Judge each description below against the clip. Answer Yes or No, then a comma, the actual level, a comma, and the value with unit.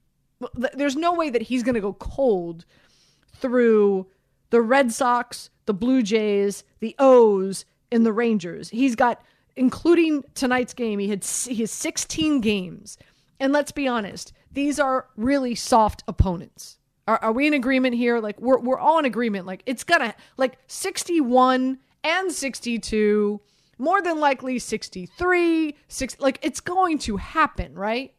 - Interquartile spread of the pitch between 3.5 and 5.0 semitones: Yes, average, 4.5 semitones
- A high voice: Yes, very high, 250 Hz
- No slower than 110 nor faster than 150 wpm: Yes, average, 145 wpm